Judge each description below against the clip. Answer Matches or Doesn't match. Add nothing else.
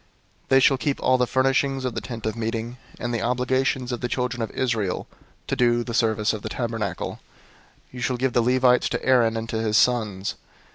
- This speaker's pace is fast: Matches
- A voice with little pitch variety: Matches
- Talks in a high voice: Doesn't match